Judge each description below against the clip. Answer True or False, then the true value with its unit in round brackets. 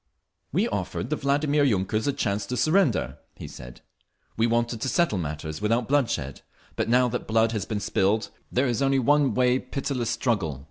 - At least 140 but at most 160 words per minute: False (175 wpm)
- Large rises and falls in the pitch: False (4.7 semitones)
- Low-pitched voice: True (120 Hz)